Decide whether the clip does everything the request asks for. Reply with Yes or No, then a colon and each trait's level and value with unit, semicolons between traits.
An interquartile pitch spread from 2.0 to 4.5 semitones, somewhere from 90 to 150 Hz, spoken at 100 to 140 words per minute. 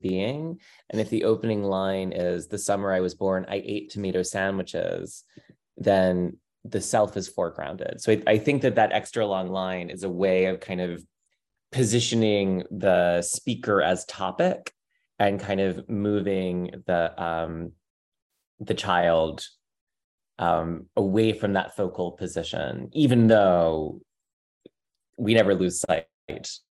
Yes: average, 2.9 semitones; very low, 95 Hz; slow, 135 wpm